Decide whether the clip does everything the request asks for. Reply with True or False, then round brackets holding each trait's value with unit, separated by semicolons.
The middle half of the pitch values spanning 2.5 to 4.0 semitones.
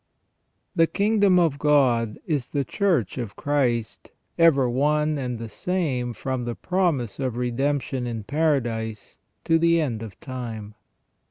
False (4.8 semitones)